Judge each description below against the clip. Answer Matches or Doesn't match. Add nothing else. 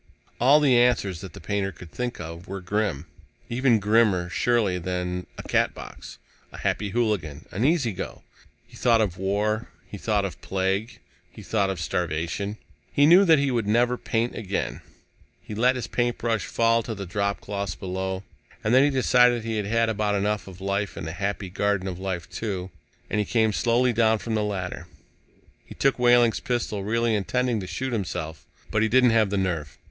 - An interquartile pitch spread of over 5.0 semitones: Doesn't match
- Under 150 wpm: Doesn't match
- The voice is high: Doesn't match